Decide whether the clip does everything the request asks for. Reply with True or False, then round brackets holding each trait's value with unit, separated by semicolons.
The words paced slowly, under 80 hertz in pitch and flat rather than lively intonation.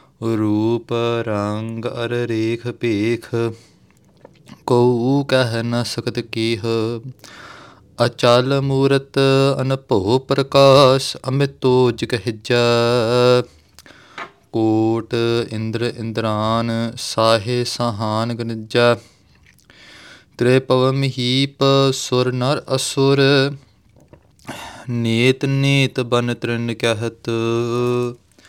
False (75 wpm; 120 Hz; 2.3 semitones)